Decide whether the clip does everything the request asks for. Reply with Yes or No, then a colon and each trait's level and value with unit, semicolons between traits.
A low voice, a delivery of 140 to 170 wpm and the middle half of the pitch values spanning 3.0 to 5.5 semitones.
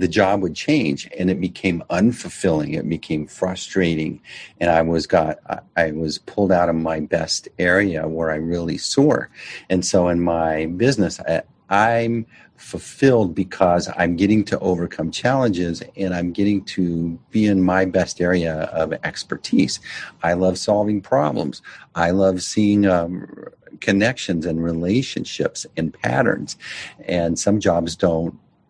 No: very low, 90 Hz; average, 145 wpm; narrow, 2.6 semitones